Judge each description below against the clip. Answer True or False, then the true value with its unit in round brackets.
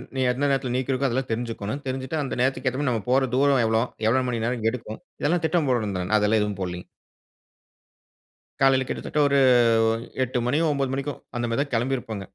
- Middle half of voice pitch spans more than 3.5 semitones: False (3.2 semitones)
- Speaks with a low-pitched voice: True (130 Hz)